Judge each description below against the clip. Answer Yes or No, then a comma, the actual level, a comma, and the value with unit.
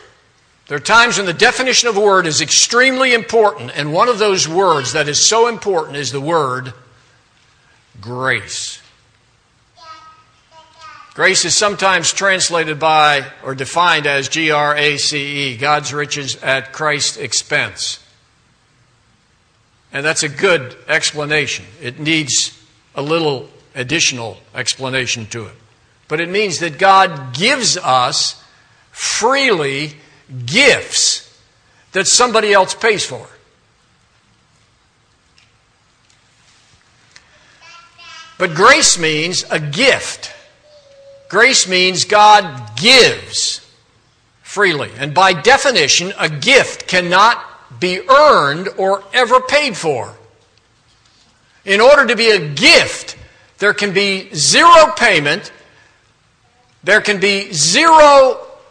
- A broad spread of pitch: Yes, wide, 8.2 semitones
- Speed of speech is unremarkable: No, slow, 110 wpm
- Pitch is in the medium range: Yes, medium, 160 Hz